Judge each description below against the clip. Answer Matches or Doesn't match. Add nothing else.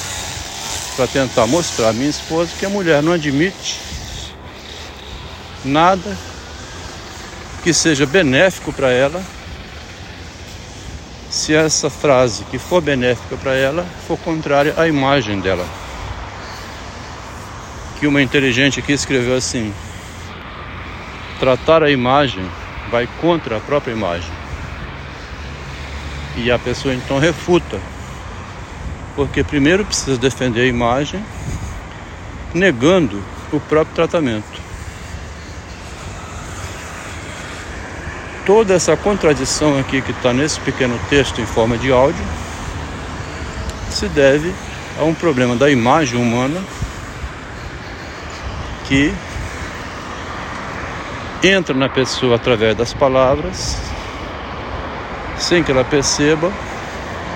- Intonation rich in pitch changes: Matches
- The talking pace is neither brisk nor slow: Doesn't match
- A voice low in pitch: Matches